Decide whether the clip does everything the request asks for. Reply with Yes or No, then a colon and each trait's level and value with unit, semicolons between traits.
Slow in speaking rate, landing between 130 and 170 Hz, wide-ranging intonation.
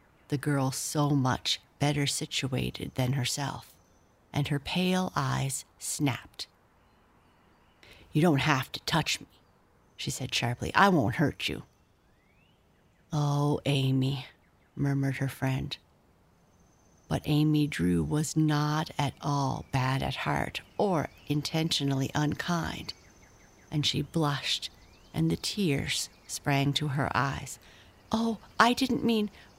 Yes: slow, 120 wpm; low, 135 Hz; wide, 6.4 semitones